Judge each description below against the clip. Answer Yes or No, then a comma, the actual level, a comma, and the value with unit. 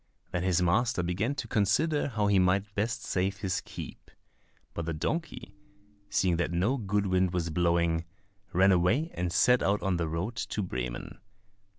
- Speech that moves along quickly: No, average, 170 wpm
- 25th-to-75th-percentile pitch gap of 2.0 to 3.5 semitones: No, average, 3.9 semitones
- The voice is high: No, very low, 95 Hz